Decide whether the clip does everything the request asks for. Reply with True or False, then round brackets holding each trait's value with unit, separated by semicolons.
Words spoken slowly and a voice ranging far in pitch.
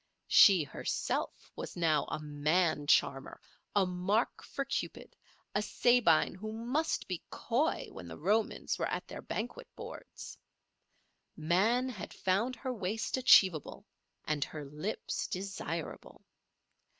True (125 wpm; 6.9 semitones)